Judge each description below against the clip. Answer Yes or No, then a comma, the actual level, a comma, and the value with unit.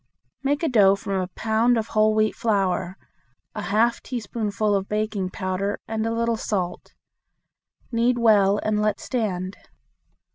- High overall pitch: Yes, high, 215 Hz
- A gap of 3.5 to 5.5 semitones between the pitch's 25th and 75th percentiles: No, average, 2.7 semitones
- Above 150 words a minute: No, average, 145 wpm